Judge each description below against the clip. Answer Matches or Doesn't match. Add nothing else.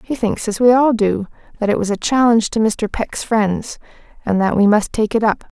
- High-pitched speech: Matches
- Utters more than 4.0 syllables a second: Matches